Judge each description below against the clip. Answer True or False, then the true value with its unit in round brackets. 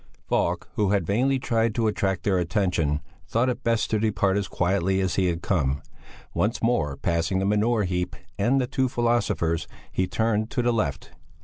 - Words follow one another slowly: False (185 wpm)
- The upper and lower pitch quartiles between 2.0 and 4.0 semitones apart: False (4.4 semitones)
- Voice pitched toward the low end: True (100 Hz)